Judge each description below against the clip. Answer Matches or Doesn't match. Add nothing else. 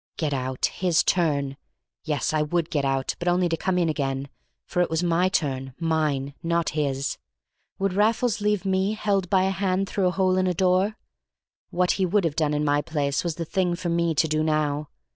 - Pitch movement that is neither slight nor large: Matches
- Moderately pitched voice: Matches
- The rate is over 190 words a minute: Matches